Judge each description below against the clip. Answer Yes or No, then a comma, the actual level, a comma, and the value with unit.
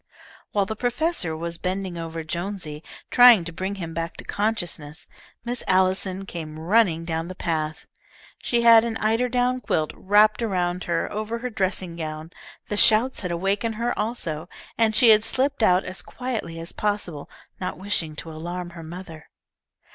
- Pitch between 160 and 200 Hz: Yes, medium, 185 Hz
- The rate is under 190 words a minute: Yes, average, 160 wpm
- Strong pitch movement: No, average, 4.9 semitones